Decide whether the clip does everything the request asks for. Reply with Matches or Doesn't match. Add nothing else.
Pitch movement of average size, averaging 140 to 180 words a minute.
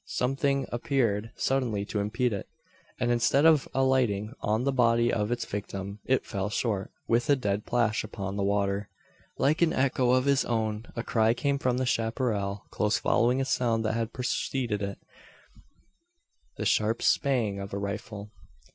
Matches